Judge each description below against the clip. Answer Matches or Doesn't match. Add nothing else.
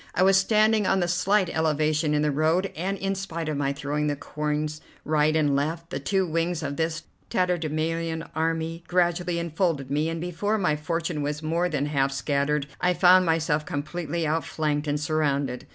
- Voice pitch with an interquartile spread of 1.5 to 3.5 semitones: Matches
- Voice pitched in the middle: Matches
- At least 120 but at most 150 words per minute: Doesn't match